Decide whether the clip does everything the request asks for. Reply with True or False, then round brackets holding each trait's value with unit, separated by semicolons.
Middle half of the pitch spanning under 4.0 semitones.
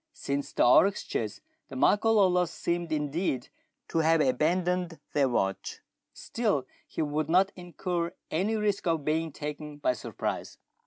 True (3.6 semitones)